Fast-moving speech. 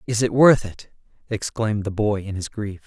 Yes: fast, 210 wpm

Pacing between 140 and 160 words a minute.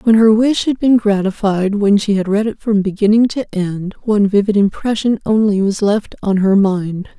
No: average, 200 wpm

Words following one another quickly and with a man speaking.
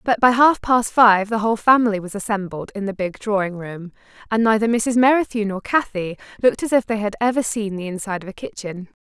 No: fast, 220 wpm; female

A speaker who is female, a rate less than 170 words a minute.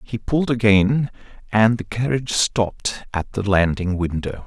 No: male; average, 150 wpm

